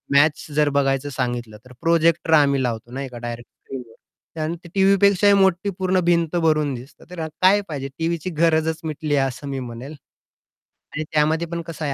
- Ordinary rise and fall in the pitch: Yes, average, 3.9 semitones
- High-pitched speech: No, medium, 155 Hz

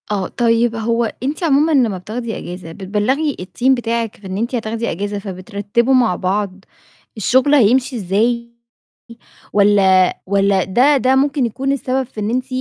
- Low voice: No, high, 230 Hz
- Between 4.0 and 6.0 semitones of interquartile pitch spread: Yes, average, 4.3 semitones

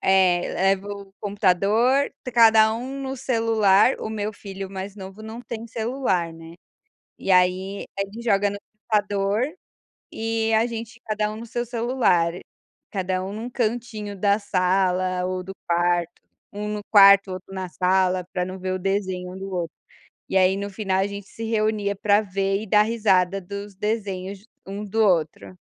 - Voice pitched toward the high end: Yes, high, 200 Hz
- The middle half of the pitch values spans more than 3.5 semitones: No, average, 2.7 semitones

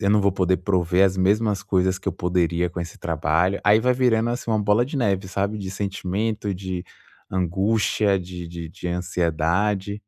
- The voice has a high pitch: No, very low, 95 Hz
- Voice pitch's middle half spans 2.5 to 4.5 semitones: Yes, average, 2.8 semitones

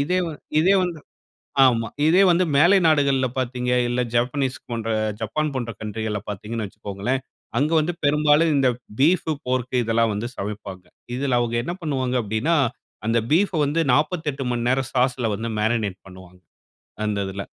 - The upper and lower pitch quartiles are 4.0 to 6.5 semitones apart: Yes, average, 5.1 semitones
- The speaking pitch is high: No, low, 125 Hz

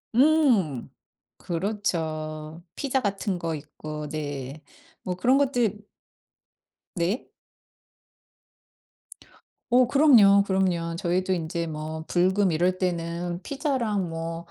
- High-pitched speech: No, medium, 180 Hz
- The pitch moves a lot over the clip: No, average, 4.2 semitones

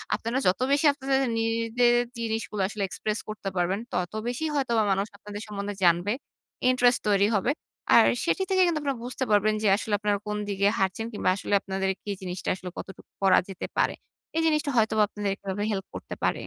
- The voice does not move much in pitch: No, average, 3.6 semitones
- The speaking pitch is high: Yes, high, 210 Hz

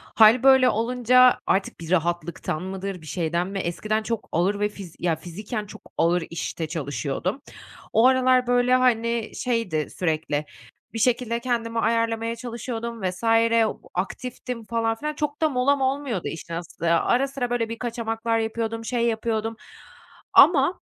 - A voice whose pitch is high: Yes, high, 225 Hz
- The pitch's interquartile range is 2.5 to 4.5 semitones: No, average, 5.1 semitones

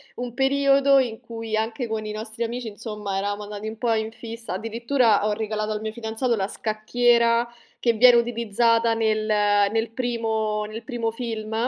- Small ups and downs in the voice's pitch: Yes, narrow, 1.6 semitones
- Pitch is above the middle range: Yes, high, 225 Hz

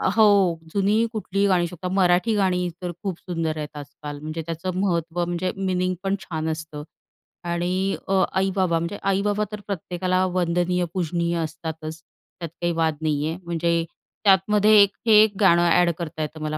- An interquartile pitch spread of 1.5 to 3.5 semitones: Yes, average, 2.7 semitones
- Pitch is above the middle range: No, medium, 175 Hz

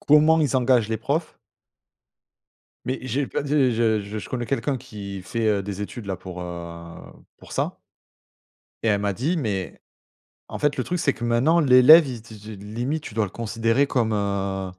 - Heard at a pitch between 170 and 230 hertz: No, low, 115 Hz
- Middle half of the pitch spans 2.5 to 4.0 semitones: No, average, 5.0 semitones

